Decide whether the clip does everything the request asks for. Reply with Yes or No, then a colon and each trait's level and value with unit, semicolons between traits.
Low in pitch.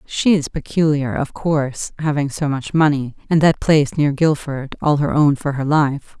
No: medium, 145 Hz